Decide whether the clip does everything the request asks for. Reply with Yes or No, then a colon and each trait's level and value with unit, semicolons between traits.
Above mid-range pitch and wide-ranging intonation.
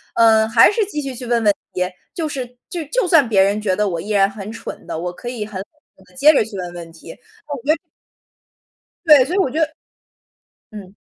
Yes: high, 225 Hz; wide, 7.0 semitones